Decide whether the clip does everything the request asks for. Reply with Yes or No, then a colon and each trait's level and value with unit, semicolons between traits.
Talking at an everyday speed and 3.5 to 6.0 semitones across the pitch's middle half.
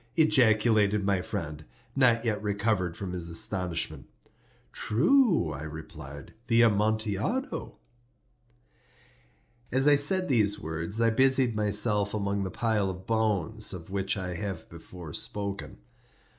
No: slow, 120 wpm; average, 4.0 semitones